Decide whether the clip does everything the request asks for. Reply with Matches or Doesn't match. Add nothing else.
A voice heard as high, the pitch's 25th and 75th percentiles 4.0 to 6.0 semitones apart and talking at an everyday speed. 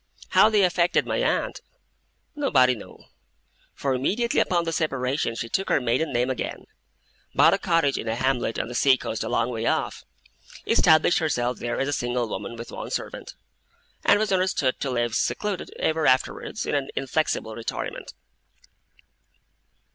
Doesn't match